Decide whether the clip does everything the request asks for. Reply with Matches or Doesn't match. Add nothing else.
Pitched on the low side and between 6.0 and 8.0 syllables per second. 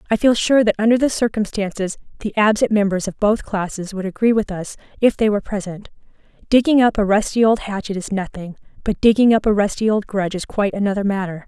Doesn't match